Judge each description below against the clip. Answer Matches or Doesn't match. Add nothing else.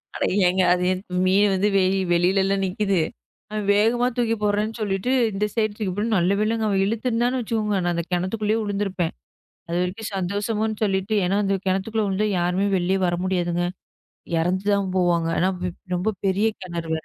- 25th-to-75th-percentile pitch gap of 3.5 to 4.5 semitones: Doesn't match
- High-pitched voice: Matches